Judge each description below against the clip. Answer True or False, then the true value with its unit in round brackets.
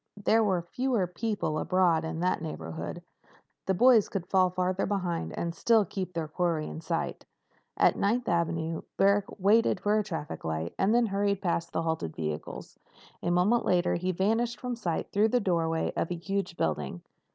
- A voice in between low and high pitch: True (180 Hz)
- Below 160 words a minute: False (175 wpm)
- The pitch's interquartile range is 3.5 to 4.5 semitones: True (3.9 semitones)